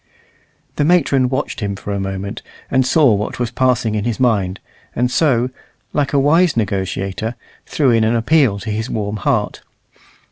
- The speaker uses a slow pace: No, average, 170 wpm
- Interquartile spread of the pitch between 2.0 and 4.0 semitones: No, average, 4.6 semitones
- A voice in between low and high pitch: No, low, 115 Hz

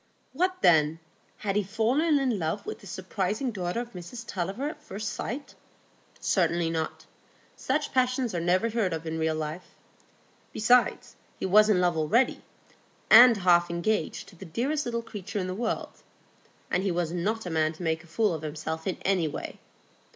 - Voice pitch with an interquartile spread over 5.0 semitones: Yes, wide, 5.4 semitones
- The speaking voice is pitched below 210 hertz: Yes, high, 190 Hz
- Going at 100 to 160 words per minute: No, average, 180 wpm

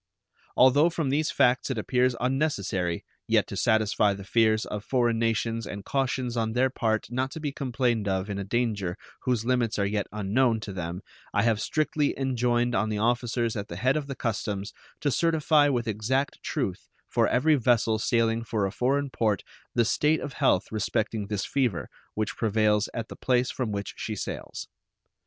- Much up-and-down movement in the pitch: No, average, 3.6 semitones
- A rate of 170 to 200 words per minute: Yes, average, 185 wpm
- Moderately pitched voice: No, low, 115 Hz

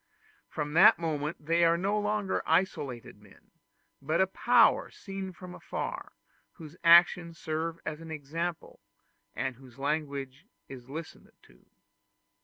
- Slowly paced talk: Yes, slow, 130 wpm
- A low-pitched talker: No, medium, 160 Hz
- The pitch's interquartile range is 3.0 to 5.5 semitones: Yes, average, 3.5 semitones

